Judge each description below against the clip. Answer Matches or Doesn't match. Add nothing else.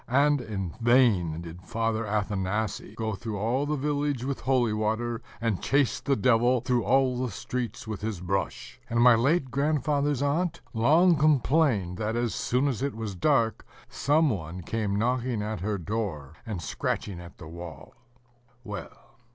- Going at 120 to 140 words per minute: Doesn't match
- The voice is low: Matches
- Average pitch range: Matches